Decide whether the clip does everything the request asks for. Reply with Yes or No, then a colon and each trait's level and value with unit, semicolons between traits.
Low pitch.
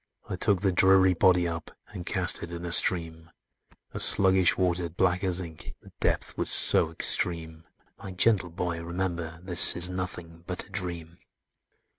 Yes: very low, 90 Hz